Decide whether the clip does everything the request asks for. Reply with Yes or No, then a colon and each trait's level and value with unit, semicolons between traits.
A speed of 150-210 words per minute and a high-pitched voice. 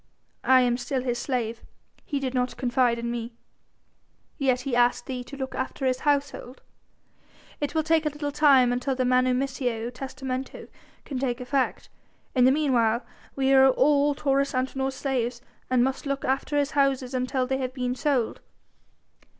Yes: average, 165 wpm; very high, 260 Hz